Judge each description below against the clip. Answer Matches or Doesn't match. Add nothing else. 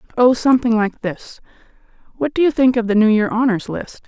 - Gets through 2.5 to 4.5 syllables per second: Doesn't match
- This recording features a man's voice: Doesn't match